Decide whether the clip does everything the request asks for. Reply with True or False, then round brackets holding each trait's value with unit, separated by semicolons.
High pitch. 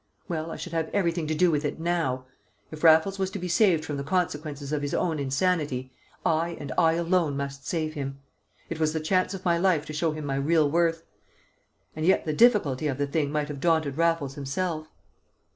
False (155 Hz)